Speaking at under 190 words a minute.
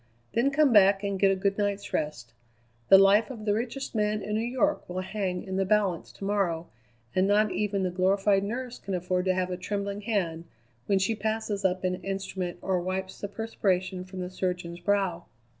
No: average, 200 wpm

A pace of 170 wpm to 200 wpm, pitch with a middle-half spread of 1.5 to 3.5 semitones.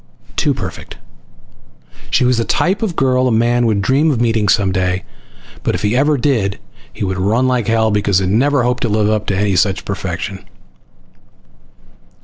No: average, 180 wpm; average, 4.3 semitones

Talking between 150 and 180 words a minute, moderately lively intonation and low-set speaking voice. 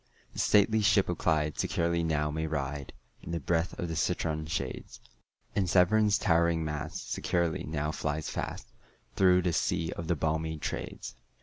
No: average, 165 wpm; narrow, 2.0 semitones; very low, 80 Hz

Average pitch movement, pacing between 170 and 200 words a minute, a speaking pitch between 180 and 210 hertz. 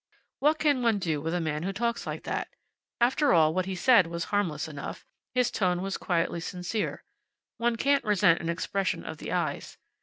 No: wide, 5.8 semitones; average, 190 wpm; high, 190 Hz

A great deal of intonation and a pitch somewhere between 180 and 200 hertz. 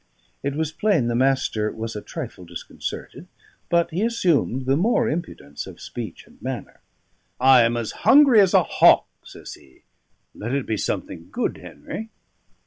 No: wide, 7.4 semitones; low, 135 Hz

